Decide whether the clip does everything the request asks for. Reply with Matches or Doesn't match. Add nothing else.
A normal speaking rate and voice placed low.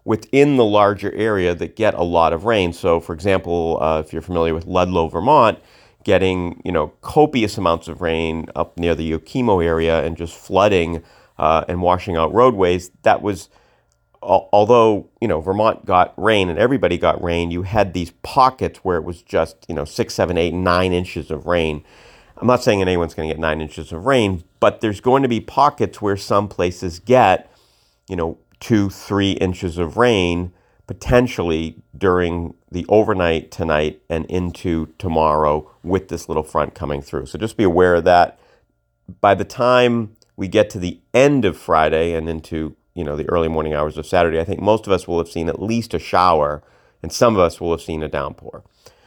Matches